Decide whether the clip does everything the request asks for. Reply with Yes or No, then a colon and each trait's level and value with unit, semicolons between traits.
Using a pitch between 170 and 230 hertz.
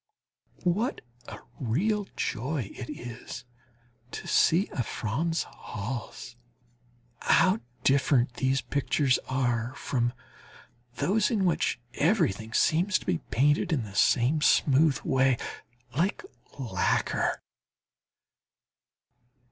No: low, 135 Hz